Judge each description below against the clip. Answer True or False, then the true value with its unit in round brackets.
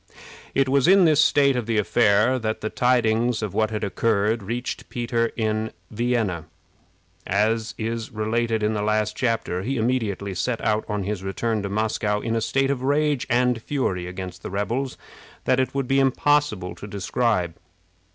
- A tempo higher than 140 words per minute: True (170 wpm)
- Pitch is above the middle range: False (115 Hz)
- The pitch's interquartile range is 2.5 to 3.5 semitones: True (3.2 semitones)